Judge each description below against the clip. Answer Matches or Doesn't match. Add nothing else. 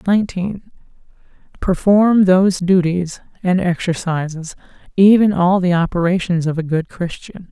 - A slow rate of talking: Matches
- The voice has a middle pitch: Matches